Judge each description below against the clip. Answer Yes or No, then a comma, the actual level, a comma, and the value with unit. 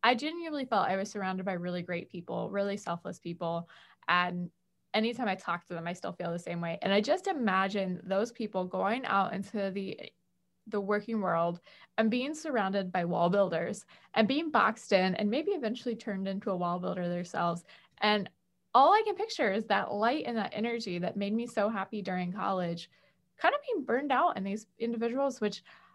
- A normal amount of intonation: Yes, average, 4.2 semitones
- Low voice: No, high, 200 Hz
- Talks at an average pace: Yes, average, 195 wpm